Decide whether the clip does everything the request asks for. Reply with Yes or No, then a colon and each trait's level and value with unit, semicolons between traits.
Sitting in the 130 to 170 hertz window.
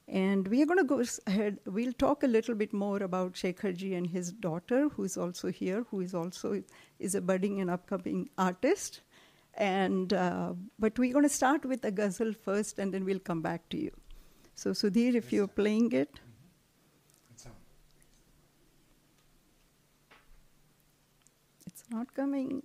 No: high, 195 Hz